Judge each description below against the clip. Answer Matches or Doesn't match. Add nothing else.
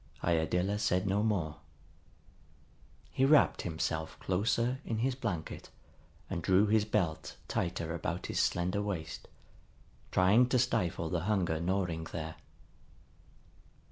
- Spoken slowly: Matches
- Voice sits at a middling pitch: Doesn't match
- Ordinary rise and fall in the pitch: Matches